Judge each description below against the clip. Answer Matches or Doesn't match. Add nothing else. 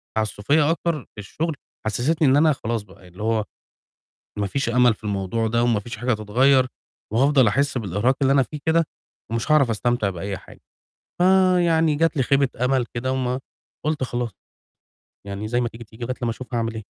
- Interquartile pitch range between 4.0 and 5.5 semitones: Matches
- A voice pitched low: Matches